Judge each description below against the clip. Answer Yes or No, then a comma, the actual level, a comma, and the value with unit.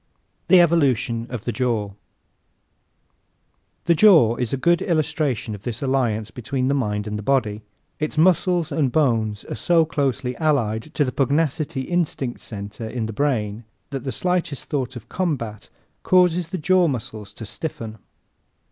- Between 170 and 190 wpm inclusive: No, average, 155 wpm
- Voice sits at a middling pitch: No, low, 130 Hz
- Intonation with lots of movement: Yes, wide, 6.0 semitones